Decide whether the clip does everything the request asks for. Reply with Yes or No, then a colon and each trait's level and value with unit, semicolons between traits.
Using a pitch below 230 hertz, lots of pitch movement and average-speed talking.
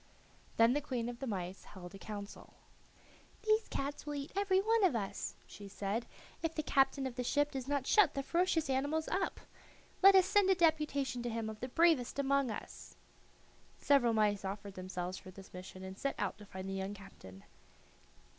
No: very high, 250 Hz; wide, 7.1 semitones; average, 195 wpm